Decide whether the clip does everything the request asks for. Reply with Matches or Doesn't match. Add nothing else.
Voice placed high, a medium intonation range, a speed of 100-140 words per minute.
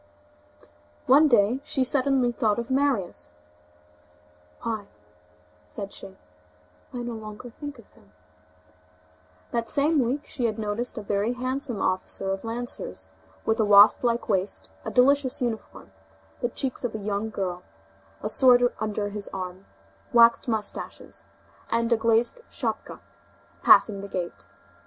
Matches